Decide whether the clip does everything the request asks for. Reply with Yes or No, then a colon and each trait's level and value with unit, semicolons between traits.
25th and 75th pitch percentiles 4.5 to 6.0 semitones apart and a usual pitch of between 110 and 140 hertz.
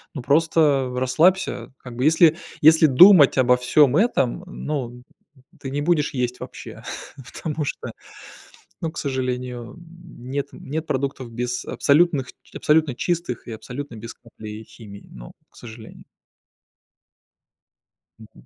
No: average, 4.1 semitones; low, 135 Hz